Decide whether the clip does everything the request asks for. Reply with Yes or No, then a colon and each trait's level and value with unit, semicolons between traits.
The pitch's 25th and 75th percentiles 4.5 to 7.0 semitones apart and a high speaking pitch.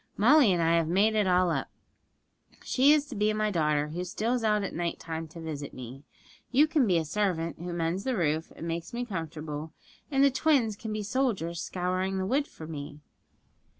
No: average, 5.2 semitones; medium, 180 Hz